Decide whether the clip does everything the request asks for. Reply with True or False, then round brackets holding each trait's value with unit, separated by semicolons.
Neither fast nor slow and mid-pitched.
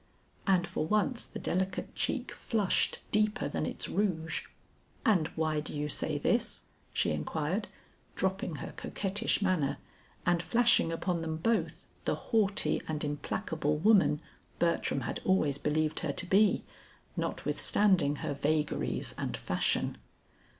False (130 wpm; 170 Hz)